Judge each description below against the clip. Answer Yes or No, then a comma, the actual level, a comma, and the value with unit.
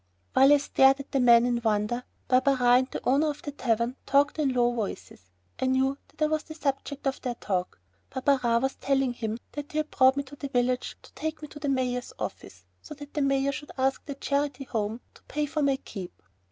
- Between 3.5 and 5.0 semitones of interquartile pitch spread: No, narrow, 2.6 semitones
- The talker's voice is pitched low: No, very high, 270 Hz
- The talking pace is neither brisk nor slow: No, fast, 225 wpm